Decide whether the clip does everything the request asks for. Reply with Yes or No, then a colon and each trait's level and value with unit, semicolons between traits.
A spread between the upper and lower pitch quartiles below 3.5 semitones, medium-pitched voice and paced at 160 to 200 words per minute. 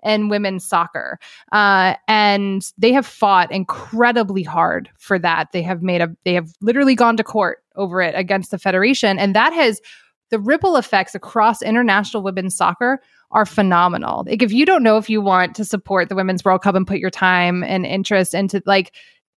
No: average, 2.9 semitones; high, 200 Hz; average, 190 wpm